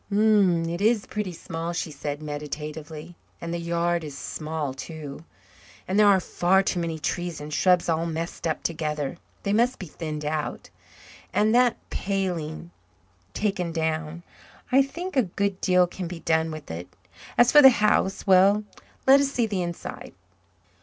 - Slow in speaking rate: No, average, 160 wpm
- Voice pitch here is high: No, medium, 170 Hz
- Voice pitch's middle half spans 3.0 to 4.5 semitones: Yes, average, 4.2 semitones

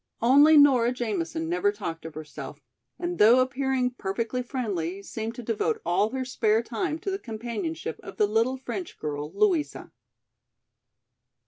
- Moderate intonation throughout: Yes, average, 4.9 semitones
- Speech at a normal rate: Yes, average, 145 wpm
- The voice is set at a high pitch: Yes, high, 230 Hz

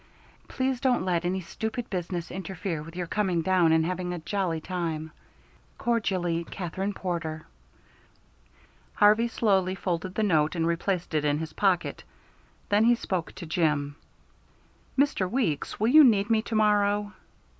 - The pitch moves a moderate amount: Yes, average, 3.8 semitones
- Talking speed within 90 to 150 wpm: Yes, average, 145 wpm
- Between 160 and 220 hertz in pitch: Yes, medium, 185 Hz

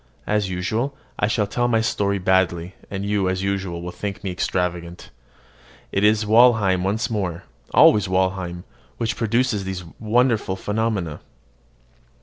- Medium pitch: No, low, 100 Hz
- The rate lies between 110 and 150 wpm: Yes, slow, 135 wpm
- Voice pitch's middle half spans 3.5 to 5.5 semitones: No, average, 2.9 semitones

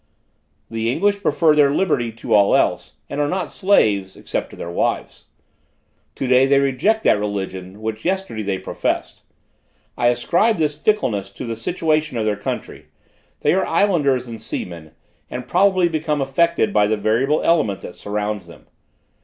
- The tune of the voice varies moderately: No, wide, 7.7 semitones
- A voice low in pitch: Yes, low, 130 Hz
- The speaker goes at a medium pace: Yes, average, 160 wpm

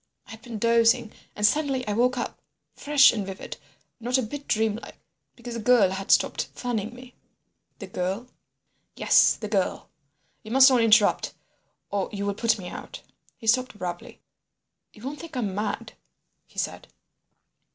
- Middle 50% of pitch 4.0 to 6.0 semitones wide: No, average, 3.3 semitones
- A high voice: Yes, high, 225 Hz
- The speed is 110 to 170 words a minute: Yes, average, 150 wpm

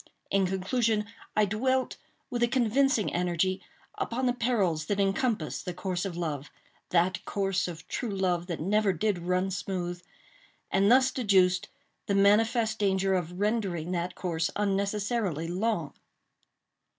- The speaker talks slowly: Yes, slow, 130 wpm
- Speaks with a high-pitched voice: Yes, high, 195 Hz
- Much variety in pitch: No, average, 3.6 semitones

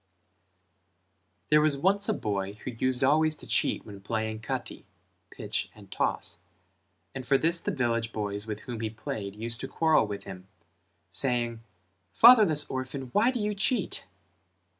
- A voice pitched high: No, low, 125 Hz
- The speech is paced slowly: No, average, 155 wpm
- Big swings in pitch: Yes, wide, 6.1 semitones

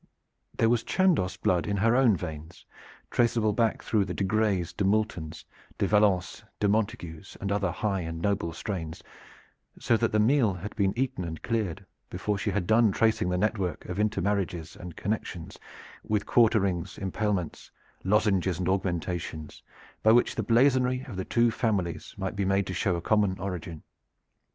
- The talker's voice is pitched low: Yes, low, 100 Hz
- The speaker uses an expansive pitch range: No, average, 3.5 semitones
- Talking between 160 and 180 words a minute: Yes, average, 165 wpm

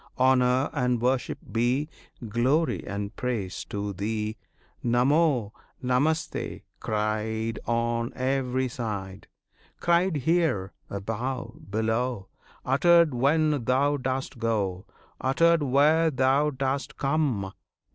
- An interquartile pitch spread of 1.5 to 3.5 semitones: No, average, 4.2 semitones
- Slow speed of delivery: Yes, slow, 95 wpm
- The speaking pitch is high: No, low, 125 Hz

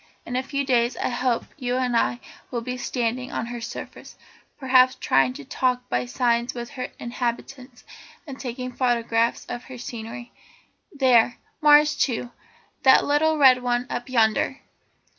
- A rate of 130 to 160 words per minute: Yes, average, 155 wpm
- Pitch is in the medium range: No, high, 245 Hz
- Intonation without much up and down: Yes, narrow, 1.5 semitones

